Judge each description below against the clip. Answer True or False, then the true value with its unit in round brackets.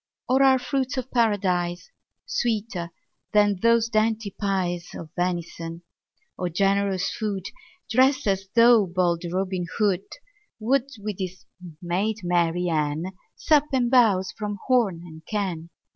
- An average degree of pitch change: True (4.7 semitones)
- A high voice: True (195 Hz)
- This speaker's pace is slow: True (130 wpm)